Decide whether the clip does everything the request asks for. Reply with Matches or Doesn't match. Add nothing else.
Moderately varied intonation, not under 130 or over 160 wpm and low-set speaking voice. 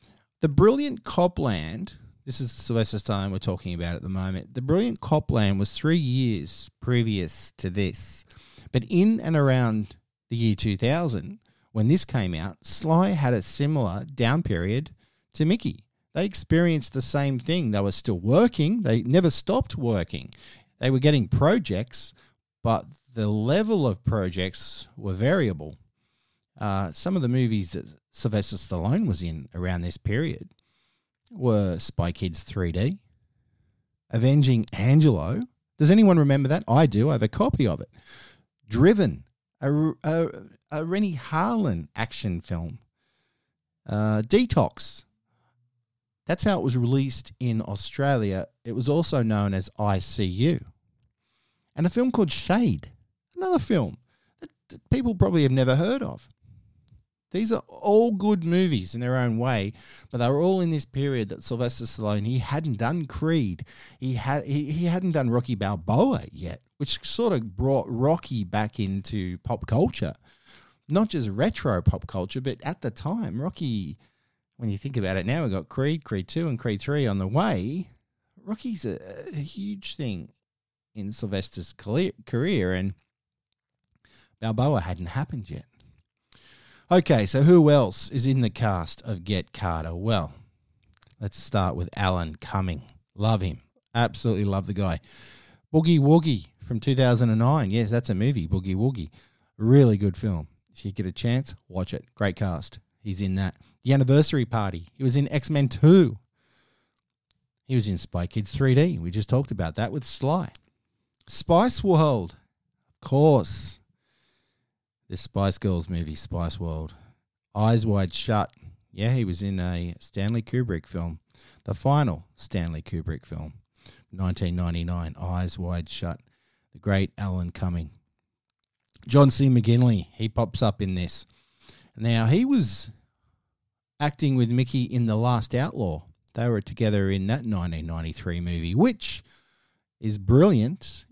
Doesn't match